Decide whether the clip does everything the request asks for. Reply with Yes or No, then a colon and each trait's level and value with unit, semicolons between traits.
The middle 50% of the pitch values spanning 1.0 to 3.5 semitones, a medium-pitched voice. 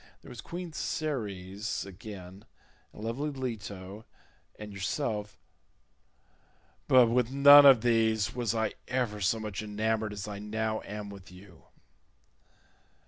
No: average, 3.1 semitones; low, 110 Hz